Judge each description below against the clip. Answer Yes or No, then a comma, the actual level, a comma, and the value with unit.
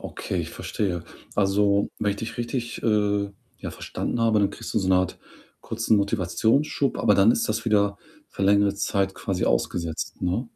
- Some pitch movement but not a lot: No, narrow, 2.2 semitones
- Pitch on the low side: Yes, low, 100 Hz